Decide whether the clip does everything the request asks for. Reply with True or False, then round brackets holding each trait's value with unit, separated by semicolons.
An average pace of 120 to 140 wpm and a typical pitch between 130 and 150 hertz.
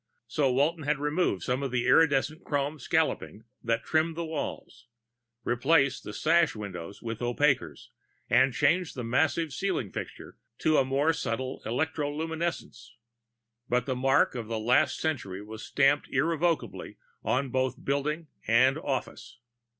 True (135 wpm; 140 Hz)